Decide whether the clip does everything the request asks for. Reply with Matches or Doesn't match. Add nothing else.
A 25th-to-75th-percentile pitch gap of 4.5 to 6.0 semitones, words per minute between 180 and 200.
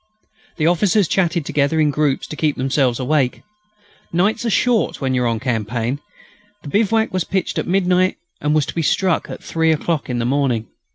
Matches